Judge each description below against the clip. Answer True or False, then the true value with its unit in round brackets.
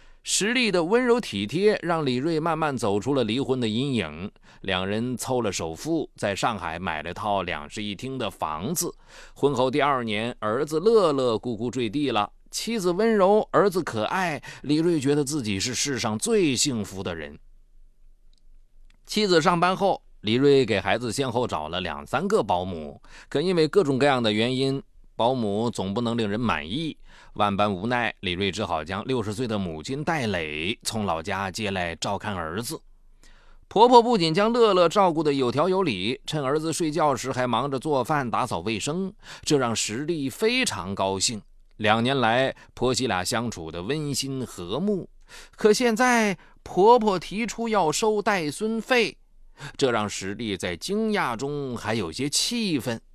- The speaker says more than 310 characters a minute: False (240 characters per minute)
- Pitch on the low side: True (130 Hz)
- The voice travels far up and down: True (8.2 semitones)